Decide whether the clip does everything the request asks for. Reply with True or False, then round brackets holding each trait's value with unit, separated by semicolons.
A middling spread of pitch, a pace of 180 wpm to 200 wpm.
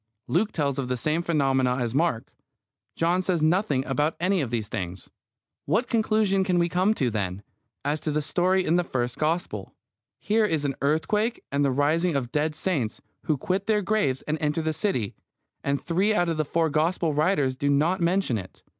True (5.0 semitones; 195 wpm)